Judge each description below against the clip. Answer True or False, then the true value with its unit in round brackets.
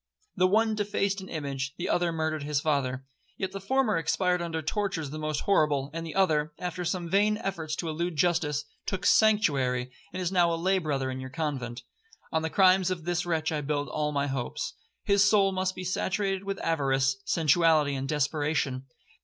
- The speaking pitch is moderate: True (165 Hz)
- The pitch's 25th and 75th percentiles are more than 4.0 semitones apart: True (4.4 semitones)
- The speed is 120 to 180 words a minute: False (190 wpm)